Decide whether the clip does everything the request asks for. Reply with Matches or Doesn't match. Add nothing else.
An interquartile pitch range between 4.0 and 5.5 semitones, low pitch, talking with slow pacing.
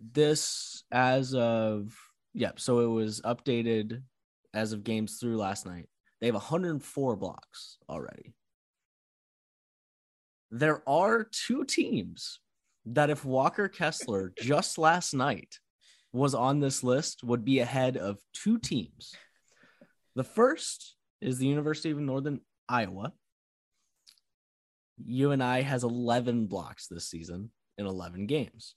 Matches